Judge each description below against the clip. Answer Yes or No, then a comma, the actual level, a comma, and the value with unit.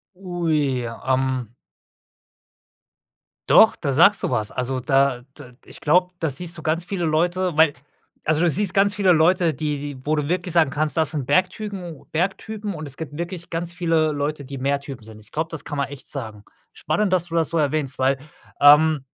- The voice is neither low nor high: Yes, medium, 155 Hz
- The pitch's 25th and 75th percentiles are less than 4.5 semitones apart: Yes, average, 4.0 semitones